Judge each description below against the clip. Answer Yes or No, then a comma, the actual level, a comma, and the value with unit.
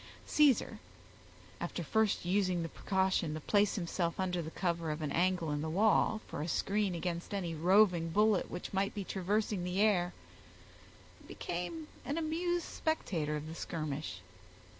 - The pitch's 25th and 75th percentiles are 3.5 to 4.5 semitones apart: Yes, average, 3.9 semitones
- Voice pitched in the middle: Yes, medium, 180 Hz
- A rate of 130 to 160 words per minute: Yes, average, 155 wpm